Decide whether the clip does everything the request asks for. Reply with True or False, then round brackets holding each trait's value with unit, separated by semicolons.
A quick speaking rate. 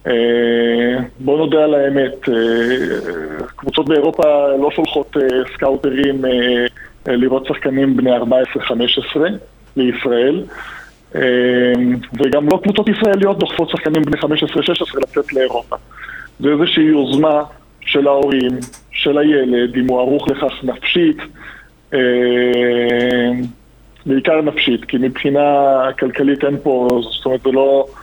False (105 wpm)